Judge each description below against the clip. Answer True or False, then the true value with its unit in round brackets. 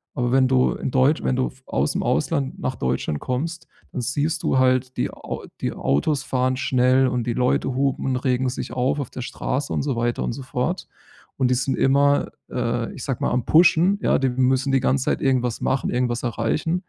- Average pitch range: False (1.7 semitones)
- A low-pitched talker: True (130 Hz)